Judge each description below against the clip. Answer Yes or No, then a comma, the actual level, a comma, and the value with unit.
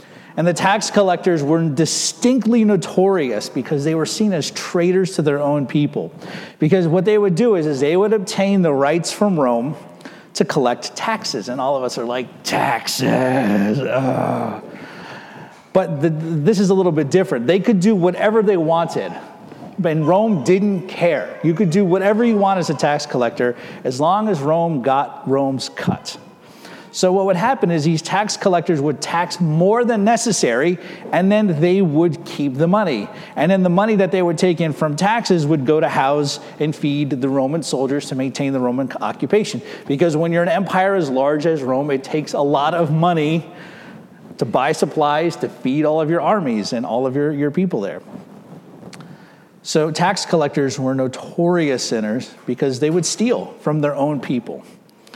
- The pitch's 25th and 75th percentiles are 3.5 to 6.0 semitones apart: Yes, average, 4.6 semitones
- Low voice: No, medium, 170 Hz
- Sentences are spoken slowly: No, average, 180 wpm